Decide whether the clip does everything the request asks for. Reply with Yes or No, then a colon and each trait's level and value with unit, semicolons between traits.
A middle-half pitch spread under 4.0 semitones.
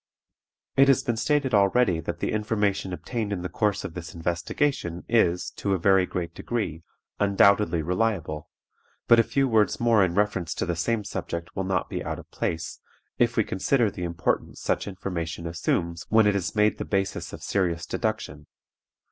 No: average, 4.5 semitones